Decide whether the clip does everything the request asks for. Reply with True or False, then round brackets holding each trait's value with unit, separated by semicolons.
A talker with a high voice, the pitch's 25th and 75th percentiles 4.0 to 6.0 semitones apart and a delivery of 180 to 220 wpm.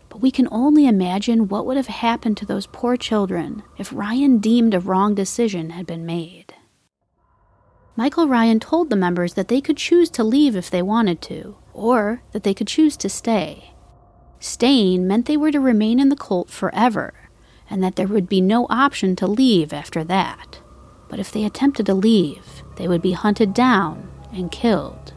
True (215 Hz; 4.8 semitones; 185 wpm)